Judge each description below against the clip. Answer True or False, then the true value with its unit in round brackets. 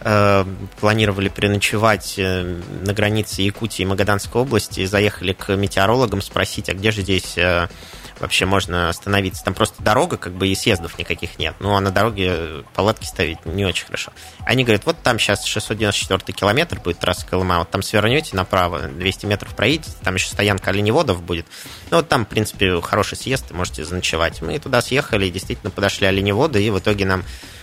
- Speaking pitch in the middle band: False (100 Hz)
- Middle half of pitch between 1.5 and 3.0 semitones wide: True (2.6 semitones)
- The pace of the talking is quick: True (170 wpm)